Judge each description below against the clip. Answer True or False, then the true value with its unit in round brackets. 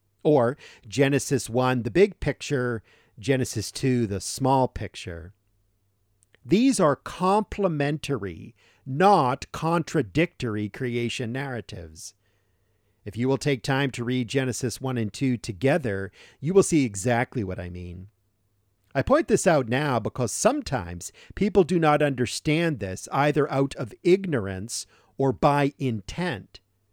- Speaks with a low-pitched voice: True (125 Hz)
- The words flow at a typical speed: False (125 wpm)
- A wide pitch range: True (5.8 semitones)